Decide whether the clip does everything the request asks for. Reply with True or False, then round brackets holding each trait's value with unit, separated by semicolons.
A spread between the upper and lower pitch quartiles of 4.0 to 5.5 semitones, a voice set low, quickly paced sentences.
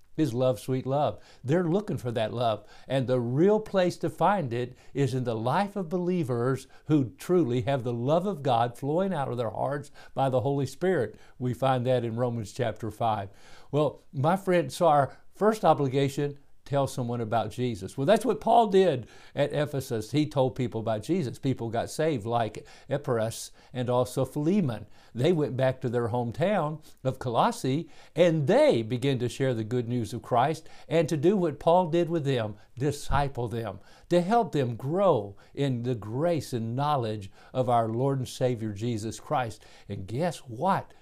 False (4.9 semitones; 130 Hz; 180 wpm)